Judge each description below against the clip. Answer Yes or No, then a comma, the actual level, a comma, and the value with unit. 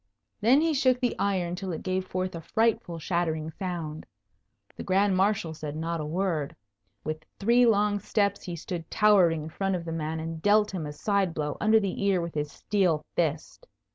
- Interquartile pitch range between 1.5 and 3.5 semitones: No, average, 4.0 semitones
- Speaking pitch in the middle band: Yes, medium, 180 Hz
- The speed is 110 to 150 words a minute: No, average, 195 wpm